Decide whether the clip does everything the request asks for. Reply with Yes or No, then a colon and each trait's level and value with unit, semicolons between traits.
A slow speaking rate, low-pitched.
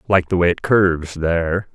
No: fast, 205 wpm; very low, 90 Hz